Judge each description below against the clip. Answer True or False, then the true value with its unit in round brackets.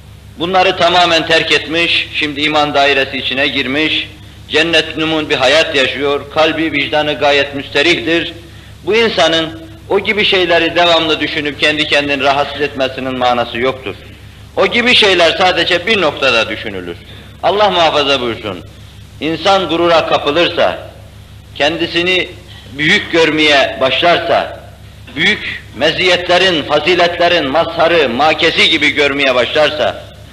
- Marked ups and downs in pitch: False (4.3 semitones)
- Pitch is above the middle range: False (150 Hz)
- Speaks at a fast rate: False (110 wpm)